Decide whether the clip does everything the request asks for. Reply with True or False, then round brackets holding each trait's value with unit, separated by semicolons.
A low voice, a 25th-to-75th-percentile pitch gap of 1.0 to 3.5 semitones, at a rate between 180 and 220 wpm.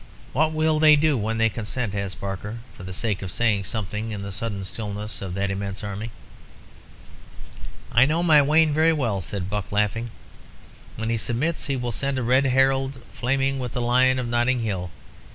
False (115 Hz; 4.7 semitones; 190 wpm)